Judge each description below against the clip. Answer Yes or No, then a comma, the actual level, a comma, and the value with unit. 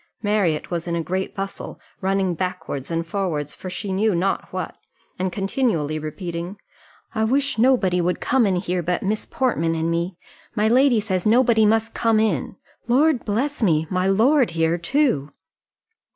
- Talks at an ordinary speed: Yes, average, 165 wpm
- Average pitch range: Yes, average, 4.7 semitones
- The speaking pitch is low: No, high, 190 Hz